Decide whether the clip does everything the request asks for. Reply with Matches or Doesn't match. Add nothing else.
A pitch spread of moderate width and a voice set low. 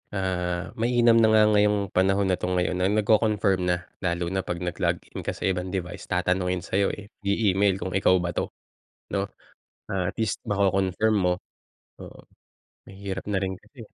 Doesn't match